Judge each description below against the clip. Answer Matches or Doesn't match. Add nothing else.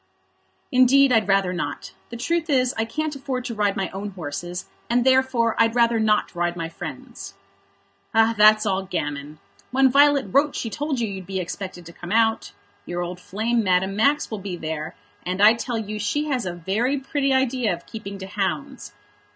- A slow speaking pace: Doesn't match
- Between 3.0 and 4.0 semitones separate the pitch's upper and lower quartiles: Doesn't match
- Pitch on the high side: Matches